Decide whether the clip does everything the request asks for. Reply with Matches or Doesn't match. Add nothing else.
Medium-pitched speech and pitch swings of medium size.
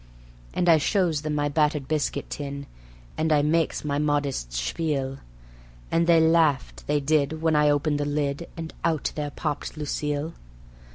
Doesn't match